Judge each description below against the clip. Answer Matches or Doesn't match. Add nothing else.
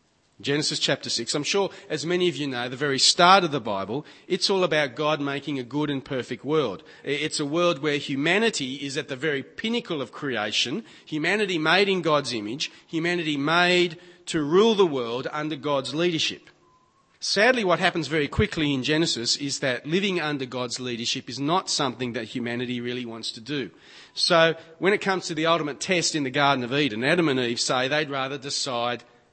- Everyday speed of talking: Matches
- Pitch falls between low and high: Matches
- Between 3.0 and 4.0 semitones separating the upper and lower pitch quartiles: Doesn't match